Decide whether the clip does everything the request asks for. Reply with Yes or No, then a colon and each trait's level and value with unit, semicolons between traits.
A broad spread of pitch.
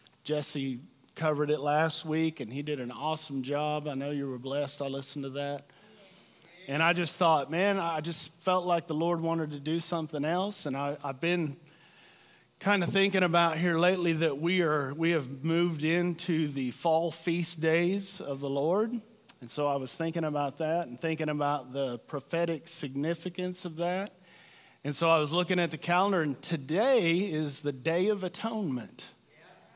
No: average, 3.1 semitones